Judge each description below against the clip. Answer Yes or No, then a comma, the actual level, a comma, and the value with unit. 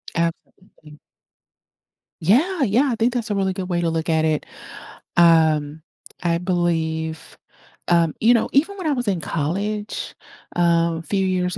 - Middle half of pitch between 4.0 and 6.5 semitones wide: Yes, average, 4.5 semitones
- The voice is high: No, medium, 175 Hz